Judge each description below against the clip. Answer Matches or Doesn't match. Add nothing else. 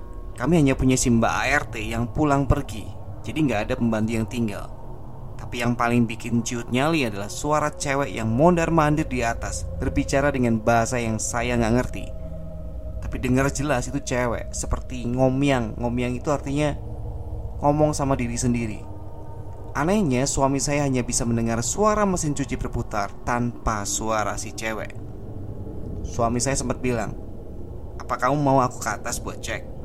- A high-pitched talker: Doesn't match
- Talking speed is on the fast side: Matches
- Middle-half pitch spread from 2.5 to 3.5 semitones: Doesn't match